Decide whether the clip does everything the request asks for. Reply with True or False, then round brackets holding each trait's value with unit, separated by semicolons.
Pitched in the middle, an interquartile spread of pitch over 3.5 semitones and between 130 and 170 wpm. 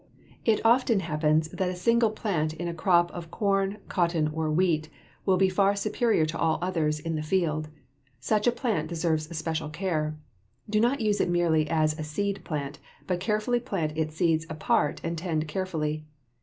False (170 Hz; 4.1 semitones; 180 wpm)